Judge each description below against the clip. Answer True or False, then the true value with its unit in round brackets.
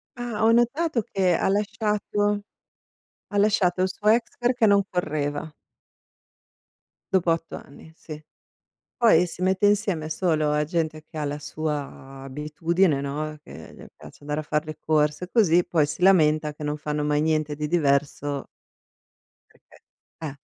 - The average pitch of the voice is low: False (160 Hz)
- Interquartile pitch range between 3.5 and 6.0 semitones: True (4.8 semitones)